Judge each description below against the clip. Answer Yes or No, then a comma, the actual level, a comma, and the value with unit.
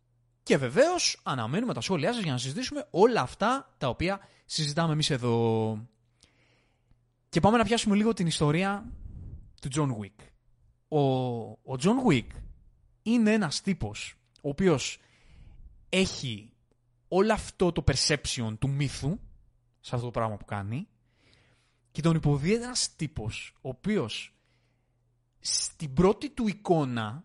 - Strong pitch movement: Yes, wide, 7.4 semitones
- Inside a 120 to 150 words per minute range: Yes, average, 130 wpm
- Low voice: Yes, low, 130 Hz